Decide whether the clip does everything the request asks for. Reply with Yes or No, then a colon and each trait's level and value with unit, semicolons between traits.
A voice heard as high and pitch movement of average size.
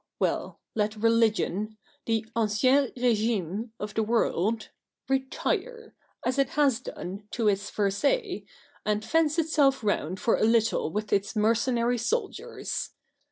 Yes: high, 225 Hz; average, 4.0 semitones